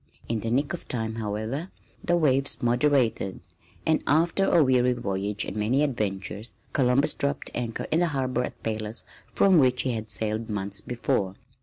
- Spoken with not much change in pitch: No, average, 4.5 semitones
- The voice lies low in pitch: Yes, low, 120 Hz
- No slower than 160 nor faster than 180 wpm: Yes, average, 165 wpm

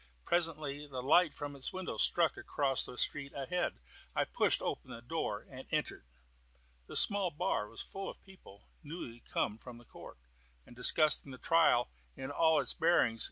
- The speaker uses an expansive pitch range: No, average, 4.9 semitones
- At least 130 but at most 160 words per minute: No, average, 170 wpm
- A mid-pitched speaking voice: Yes, medium, 145 Hz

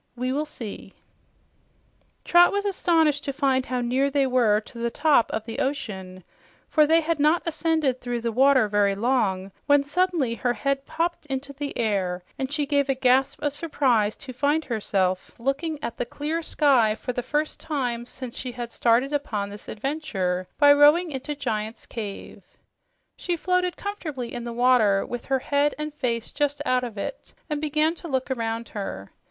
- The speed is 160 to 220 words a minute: Yes, average, 180 wpm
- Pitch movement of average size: Yes, average, 4.3 semitones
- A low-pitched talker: No, very high, 265 Hz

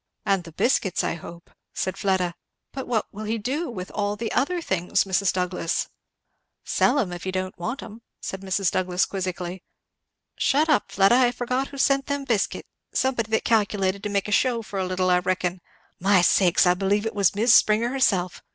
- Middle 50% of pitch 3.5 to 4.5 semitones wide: Yes, average, 4.2 semitones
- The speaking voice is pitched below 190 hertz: No, high, 200 Hz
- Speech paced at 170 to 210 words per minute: Yes, average, 195 wpm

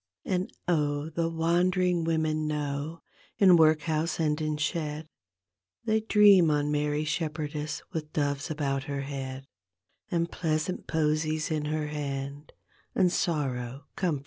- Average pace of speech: No, slow, 125 wpm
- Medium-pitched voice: Yes, medium, 155 Hz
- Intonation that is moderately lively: No, narrow, 2.1 semitones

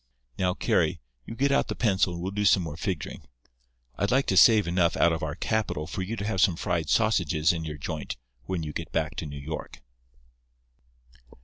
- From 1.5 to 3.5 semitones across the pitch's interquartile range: No, average, 4.1 semitones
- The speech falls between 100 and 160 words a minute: No, fast, 205 wpm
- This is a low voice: Yes, very low, 85 Hz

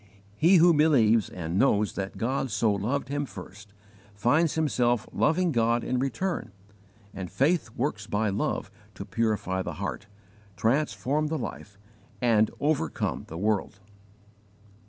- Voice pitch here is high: No, low, 115 Hz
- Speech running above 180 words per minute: No, slow, 135 wpm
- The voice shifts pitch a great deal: Yes, wide, 5.9 semitones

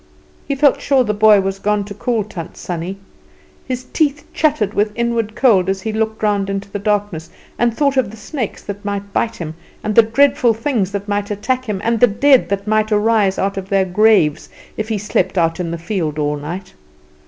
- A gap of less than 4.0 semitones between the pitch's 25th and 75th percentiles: Yes, average, 2.8 semitones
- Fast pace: Yes, fast, 210 wpm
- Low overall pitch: No, high, 210 Hz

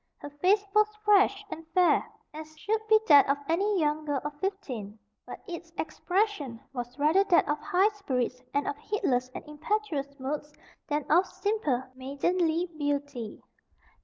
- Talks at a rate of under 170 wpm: Yes, average, 155 wpm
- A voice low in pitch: No, very high, 310 Hz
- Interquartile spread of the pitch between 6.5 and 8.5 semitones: No, wide, 5.5 semitones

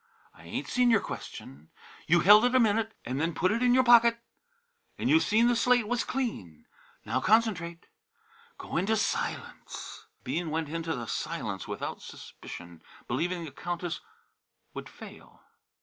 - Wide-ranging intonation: Yes, wide, 6.3 semitones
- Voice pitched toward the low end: No, high, 200 Hz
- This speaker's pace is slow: No, average, 160 wpm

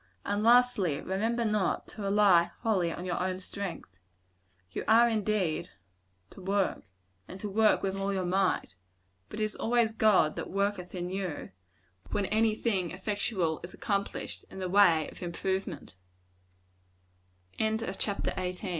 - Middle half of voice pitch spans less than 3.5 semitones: Yes, average, 2.8 semitones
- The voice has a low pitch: No, high, 195 Hz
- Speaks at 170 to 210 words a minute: No, slow, 135 wpm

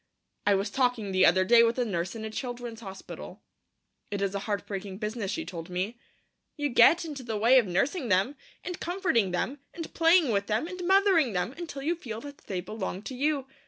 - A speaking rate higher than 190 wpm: Yes, fast, 205 wpm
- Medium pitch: No, high, 230 Hz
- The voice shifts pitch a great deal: Yes, wide, 6.5 semitones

